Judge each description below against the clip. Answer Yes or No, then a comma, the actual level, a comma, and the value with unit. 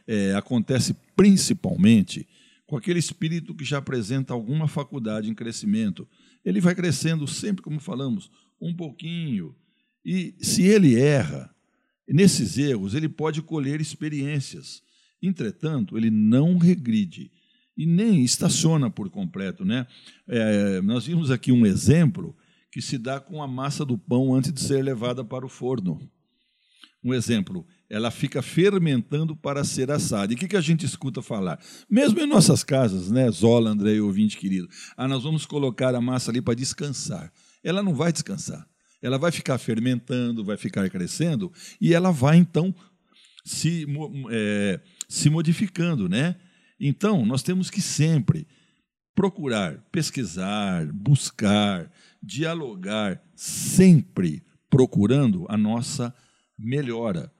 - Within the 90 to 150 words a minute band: Yes, average, 135 wpm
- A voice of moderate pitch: Yes, medium, 150 Hz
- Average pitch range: No, wide, 6.2 semitones